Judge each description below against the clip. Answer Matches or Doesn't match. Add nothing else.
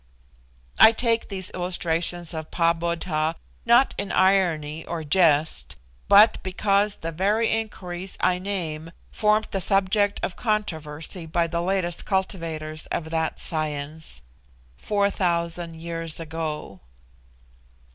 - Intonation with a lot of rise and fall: Doesn't match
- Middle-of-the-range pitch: Matches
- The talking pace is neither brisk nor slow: Doesn't match